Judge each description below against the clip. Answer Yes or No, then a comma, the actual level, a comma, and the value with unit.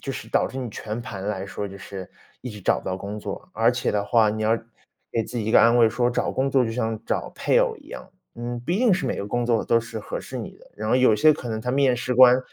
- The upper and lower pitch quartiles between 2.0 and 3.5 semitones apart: Yes, average, 2.9 semitones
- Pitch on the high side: No, low, 115 Hz